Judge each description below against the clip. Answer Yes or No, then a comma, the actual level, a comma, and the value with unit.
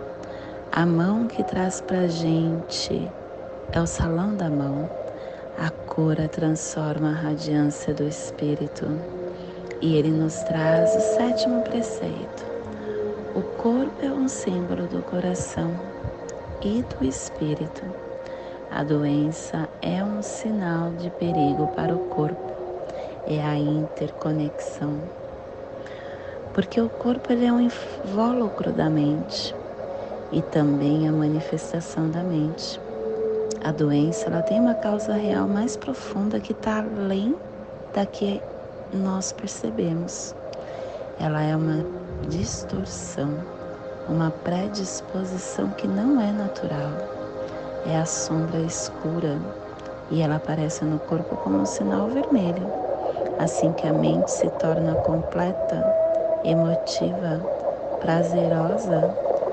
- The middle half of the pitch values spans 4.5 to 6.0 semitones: Yes, wide, 5.6 semitones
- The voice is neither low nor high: Yes, medium, 165 Hz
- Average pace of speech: No, slow, 115 wpm